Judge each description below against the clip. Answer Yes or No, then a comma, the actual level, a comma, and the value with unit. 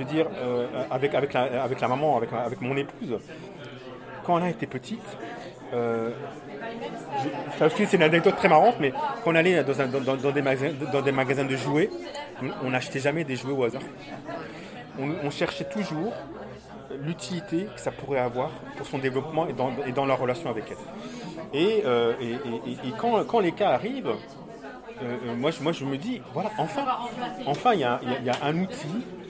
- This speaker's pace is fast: No, average, 190 wpm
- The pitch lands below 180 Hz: Yes, medium, 140 Hz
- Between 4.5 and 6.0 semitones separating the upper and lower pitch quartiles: Yes, average, 5.0 semitones